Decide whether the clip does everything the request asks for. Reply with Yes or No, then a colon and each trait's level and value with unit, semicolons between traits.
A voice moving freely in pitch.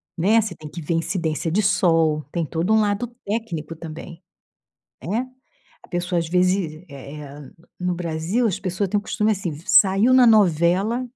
No: average, 4.1 semitones